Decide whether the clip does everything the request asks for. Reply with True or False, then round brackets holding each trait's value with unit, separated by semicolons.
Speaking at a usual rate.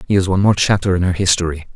False (275 wpm)